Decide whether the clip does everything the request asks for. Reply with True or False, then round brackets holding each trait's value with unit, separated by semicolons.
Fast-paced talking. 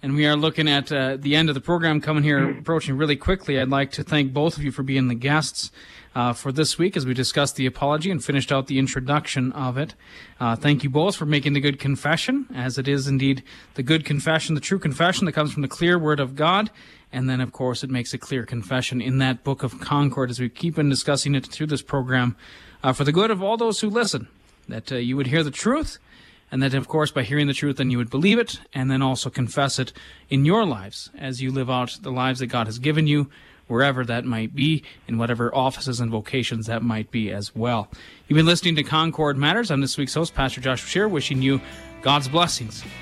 True (240 wpm)